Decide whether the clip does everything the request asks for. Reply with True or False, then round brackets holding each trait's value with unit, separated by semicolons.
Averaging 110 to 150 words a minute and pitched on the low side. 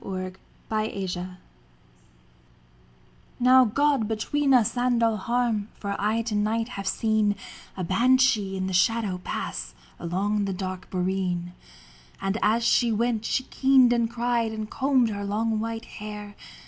False (140 wpm; 215 Hz)